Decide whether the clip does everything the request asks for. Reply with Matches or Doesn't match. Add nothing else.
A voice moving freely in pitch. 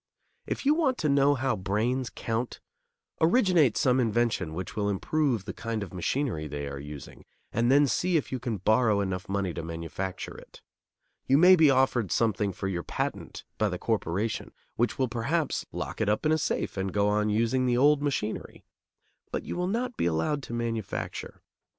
Matches